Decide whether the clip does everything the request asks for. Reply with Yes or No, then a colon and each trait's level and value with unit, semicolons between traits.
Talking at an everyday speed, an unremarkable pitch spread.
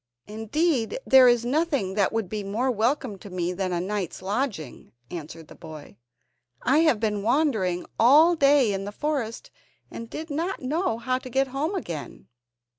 No: average, 170 wpm; wide, 6.3 semitones